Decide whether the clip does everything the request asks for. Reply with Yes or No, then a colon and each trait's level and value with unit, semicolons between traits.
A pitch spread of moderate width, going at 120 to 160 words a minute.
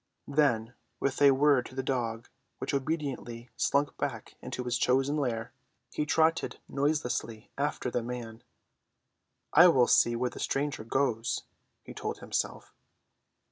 Yes: average, 3.3 semitones; average, 140 wpm